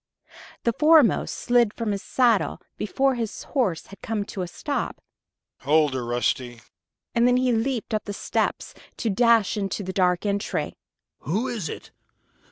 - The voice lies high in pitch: Yes, high, 210 Hz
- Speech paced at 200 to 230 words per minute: No, average, 160 wpm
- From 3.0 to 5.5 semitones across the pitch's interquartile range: Yes, average, 4.6 semitones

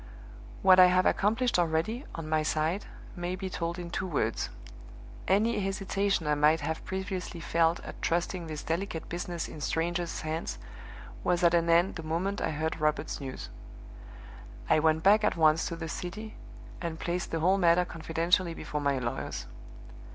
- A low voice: No, medium, 170 Hz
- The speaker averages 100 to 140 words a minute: No, average, 165 wpm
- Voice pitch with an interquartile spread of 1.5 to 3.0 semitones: Yes, narrow, 2.6 semitones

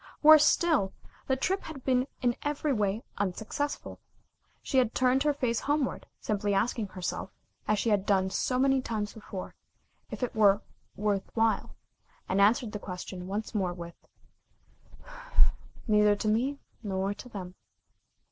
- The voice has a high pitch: Yes, high, 215 Hz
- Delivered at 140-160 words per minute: Yes, average, 145 wpm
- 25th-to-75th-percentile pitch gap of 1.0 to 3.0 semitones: No, average, 4.6 semitones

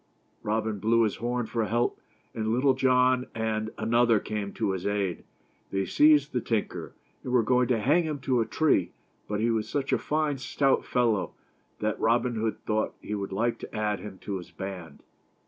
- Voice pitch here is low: Yes, low, 115 Hz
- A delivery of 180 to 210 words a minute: Yes, average, 190 wpm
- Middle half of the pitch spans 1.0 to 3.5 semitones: Yes, average, 3.2 semitones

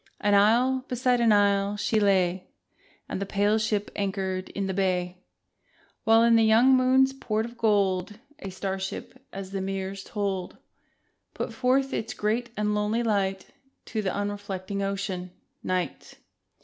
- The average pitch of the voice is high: Yes, high, 205 Hz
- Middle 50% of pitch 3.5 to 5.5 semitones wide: No, average, 2.7 semitones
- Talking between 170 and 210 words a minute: No, average, 150 wpm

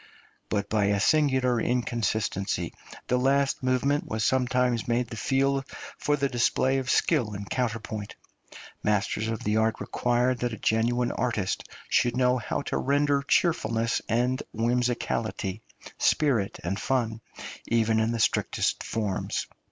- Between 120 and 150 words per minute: Yes, slow, 135 wpm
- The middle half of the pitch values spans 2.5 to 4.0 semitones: Yes, average, 2.8 semitones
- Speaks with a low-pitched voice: Yes, low, 120 Hz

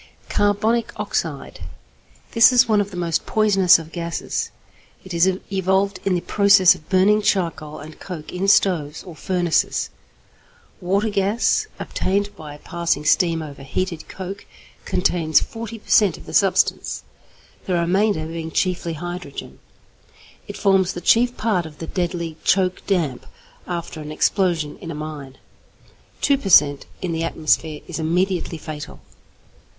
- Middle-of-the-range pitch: Yes, medium, 180 Hz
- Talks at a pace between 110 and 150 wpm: Yes, average, 145 wpm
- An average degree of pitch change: Yes, average, 3.5 semitones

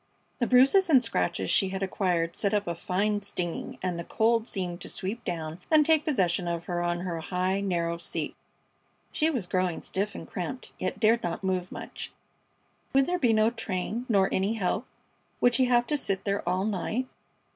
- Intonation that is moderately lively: Yes, average, 4.9 semitones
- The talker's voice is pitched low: No, high, 195 Hz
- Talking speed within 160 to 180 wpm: No, average, 190 wpm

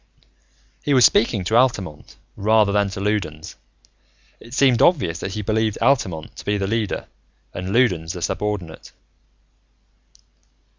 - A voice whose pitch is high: No, low, 105 Hz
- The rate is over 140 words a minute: No, slow, 135 wpm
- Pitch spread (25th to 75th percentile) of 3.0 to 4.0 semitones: Yes, average, 3.7 semitones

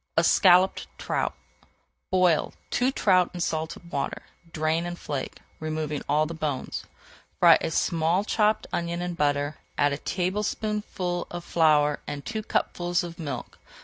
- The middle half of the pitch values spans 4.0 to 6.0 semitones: No, average, 2.9 semitones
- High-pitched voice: No, medium, 170 Hz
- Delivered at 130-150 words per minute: Yes, average, 140 wpm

